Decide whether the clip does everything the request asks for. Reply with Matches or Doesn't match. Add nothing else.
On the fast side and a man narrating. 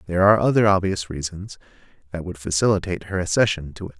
Doesn't match